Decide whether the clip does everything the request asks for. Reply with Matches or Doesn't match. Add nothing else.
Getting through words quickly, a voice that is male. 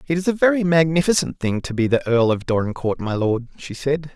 Matches